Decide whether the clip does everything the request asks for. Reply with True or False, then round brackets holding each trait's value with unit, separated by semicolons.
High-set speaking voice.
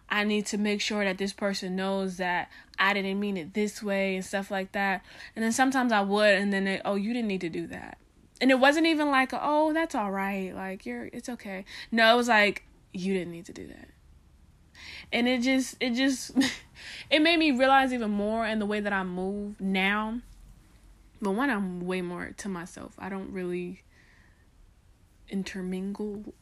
True (200 Hz)